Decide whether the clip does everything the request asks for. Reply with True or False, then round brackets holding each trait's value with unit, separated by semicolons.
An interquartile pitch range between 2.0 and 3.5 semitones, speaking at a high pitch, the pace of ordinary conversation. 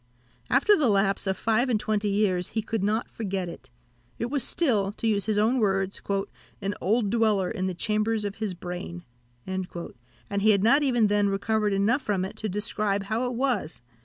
True (2.5 semitones; 210 Hz; 190 wpm)